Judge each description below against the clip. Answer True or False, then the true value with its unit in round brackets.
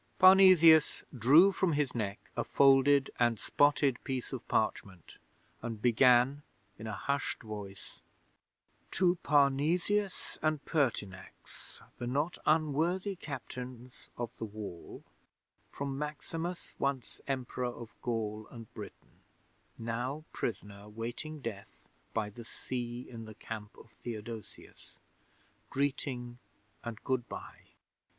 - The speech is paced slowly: True (115 wpm)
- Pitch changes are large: False (4.6 semitones)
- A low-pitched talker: True (125 Hz)